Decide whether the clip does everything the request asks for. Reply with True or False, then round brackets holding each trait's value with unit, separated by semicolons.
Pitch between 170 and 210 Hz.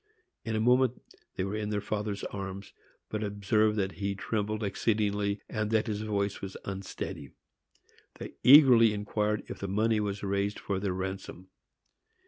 False (105 Hz)